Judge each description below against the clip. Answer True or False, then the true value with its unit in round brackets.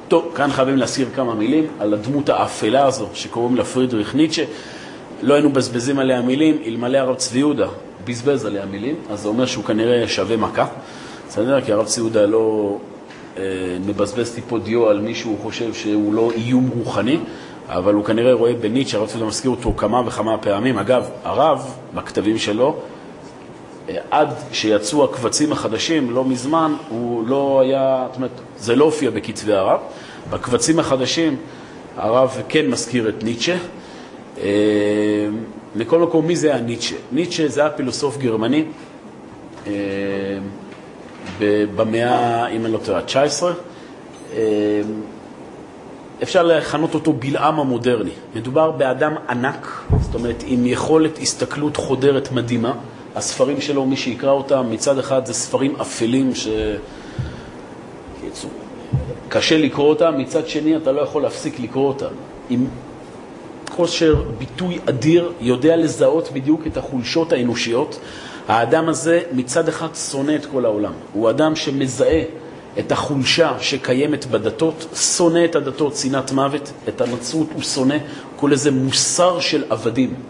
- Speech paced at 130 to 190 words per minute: True (135 wpm)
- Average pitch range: True (4.8 semitones)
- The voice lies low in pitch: True (130 Hz)